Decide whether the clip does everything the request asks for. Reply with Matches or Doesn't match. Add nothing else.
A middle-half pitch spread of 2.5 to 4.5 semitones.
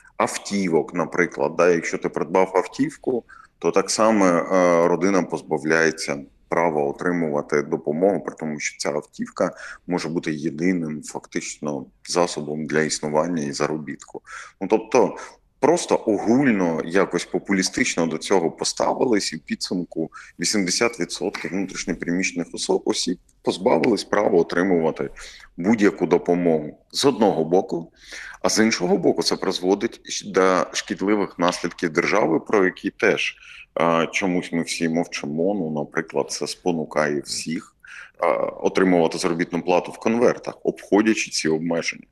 Matches